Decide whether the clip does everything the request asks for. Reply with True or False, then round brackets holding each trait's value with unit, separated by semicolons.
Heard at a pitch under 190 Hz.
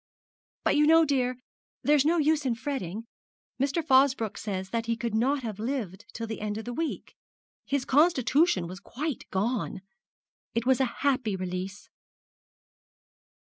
False (245 Hz)